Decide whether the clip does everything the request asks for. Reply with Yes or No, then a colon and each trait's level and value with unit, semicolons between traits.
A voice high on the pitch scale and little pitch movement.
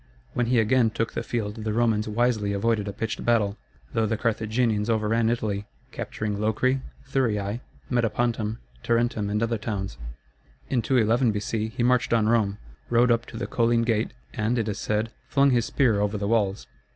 No: low, 115 Hz; narrow, 2.0 semitones